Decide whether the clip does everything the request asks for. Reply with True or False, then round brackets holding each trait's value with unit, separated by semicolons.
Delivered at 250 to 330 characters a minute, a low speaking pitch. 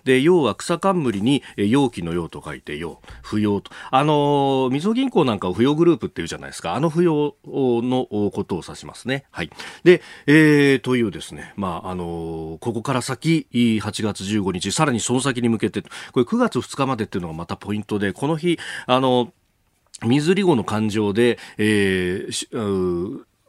True (310 characters per minute; 120 Hz)